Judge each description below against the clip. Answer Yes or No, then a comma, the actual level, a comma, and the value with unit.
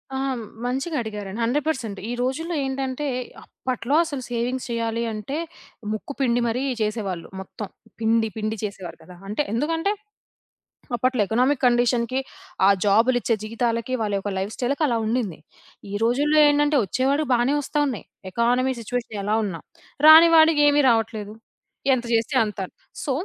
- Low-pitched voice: No, high, 240 Hz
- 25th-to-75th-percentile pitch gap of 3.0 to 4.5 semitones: Yes, average, 3.7 semitones